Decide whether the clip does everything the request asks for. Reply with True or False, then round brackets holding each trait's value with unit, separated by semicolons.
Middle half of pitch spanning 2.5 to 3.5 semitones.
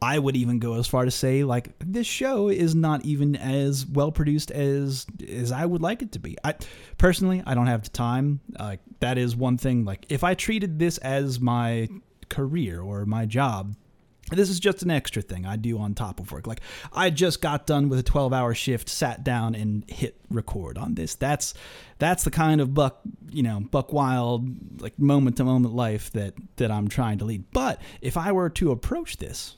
False (4.7 semitones)